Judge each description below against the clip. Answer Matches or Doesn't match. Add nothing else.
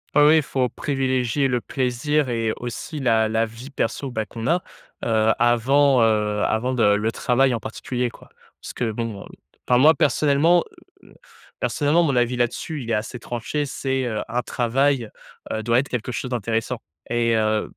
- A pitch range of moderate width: Matches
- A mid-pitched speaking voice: Doesn't match